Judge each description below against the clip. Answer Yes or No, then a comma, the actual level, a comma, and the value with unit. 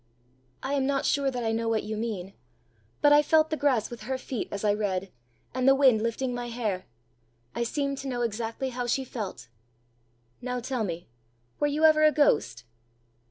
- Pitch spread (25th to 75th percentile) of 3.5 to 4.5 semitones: Yes, average, 4.0 semitones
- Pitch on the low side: No, high, 245 Hz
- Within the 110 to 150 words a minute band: No, average, 195 wpm